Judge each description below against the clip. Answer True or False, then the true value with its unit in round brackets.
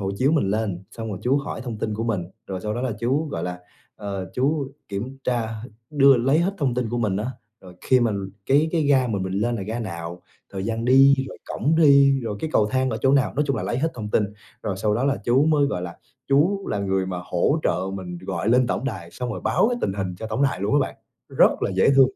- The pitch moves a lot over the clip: True (5.7 semitones)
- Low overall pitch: True (120 Hz)